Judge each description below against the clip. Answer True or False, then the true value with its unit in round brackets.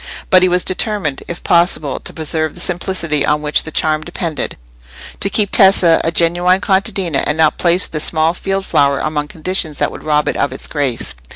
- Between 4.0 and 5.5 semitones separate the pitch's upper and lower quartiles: False (3.3 semitones)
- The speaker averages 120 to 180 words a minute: False (195 wpm)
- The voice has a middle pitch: True (165 Hz)